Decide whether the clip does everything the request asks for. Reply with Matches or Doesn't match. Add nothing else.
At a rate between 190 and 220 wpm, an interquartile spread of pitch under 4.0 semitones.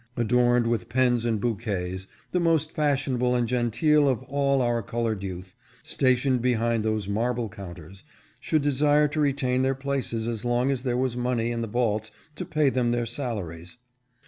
Doesn't match